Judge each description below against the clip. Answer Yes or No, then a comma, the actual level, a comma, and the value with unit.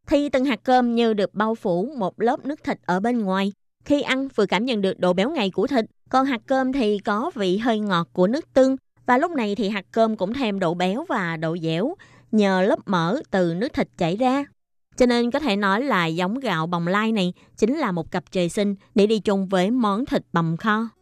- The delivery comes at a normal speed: Yes, average, 235 wpm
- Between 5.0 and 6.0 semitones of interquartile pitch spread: Yes, wide, 5.5 semitones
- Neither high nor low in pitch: No, high, 210 Hz